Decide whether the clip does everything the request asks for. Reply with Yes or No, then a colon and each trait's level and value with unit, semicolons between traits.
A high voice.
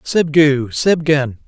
No: medium, 150 Hz